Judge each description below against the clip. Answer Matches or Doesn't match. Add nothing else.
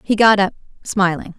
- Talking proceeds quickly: Doesn't match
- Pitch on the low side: Doesn't match